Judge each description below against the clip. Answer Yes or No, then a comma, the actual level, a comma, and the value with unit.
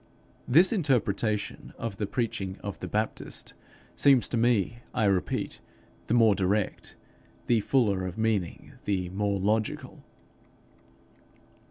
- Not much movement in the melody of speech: No, average, 3.1 semitones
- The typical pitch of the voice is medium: No, low, 105 Hz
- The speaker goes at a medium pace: No, slow, 120 wpm